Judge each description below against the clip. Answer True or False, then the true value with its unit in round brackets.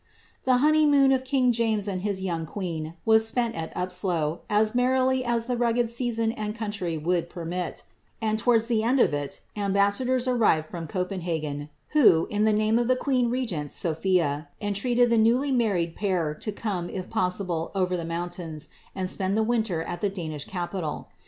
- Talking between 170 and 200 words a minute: True (175 wpm)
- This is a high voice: True (205 Hz)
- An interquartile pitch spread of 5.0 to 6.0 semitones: True (5.4 semitones)